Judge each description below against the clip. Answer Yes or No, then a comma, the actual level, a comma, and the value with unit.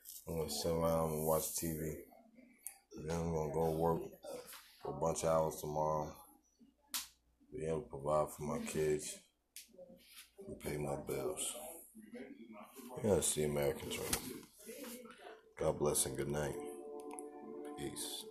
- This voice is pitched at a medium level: No, very low, 80 Hz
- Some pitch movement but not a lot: No, narrow, 2.0 semitones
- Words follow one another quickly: No, slow, 130 wpm